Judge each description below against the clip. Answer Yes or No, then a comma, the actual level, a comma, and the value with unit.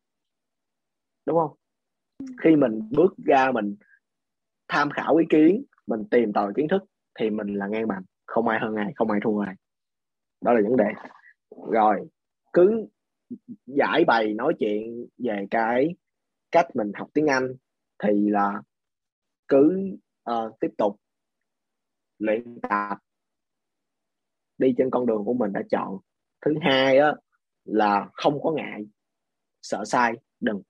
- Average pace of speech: No, slow, 140 wpm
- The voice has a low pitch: Yes, low, 115 Hz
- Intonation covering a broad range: Yes, wide, 6.6 semitones